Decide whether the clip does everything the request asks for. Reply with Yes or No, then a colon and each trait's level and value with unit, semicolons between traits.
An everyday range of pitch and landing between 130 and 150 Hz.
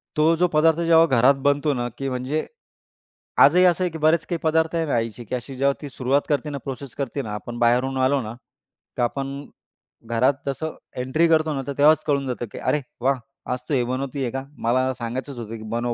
Yes: average, 3.5 semitones; low, 135 Hz